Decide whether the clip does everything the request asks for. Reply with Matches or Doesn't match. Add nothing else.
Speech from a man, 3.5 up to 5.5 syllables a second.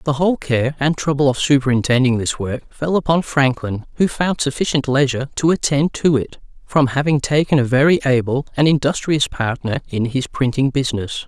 Matches